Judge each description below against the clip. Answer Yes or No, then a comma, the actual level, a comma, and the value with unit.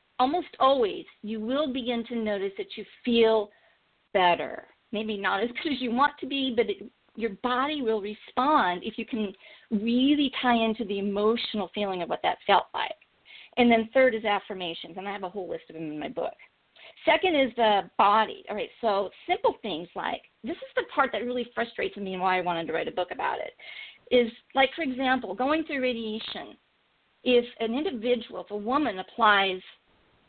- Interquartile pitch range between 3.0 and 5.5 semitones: Yes, average, 4.4 semitones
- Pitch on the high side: Yes, high, 235 Hz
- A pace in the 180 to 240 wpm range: Yes, average, 195 wpm